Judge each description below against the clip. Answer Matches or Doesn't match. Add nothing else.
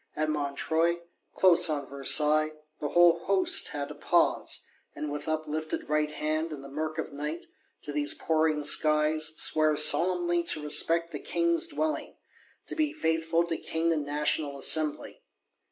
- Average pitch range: Doesn't match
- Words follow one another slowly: Doesn't match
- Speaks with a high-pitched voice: Doesn't match